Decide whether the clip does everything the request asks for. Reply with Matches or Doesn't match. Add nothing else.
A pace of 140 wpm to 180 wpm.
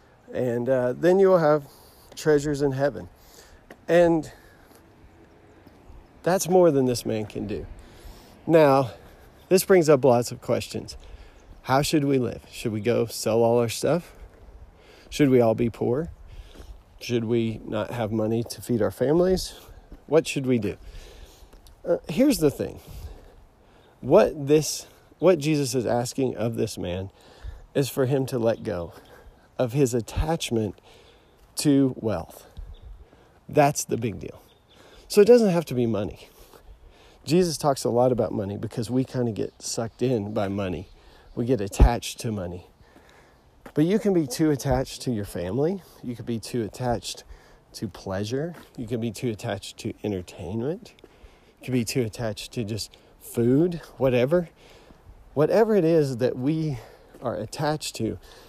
Matches